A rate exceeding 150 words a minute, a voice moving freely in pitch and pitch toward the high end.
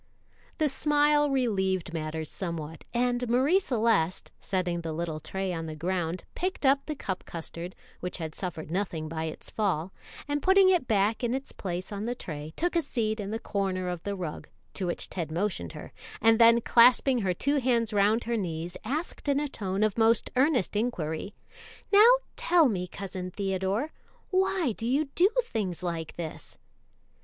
Yes: average, 175 wpm; wide, 6.6 semitones; high, 205 Hz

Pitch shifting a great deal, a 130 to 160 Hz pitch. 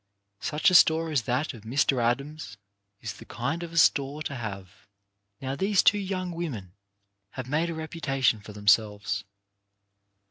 Yes: wide, 6.5 semitones; low, 135 Hz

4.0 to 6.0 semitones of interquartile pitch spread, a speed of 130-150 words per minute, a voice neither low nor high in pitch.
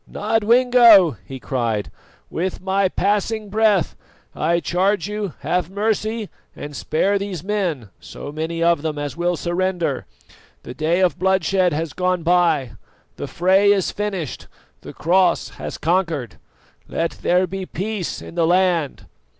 No: average, 3.6 semitones; average, 140 wpm; medium, 180 Hz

